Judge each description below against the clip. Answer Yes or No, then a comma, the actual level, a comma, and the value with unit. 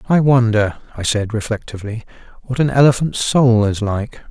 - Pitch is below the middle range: Yes, low, 115 Hz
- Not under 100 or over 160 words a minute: Yes, average, 155 wpm